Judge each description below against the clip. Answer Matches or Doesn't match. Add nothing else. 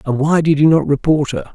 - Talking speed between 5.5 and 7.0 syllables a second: Matches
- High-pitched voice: Doesn't match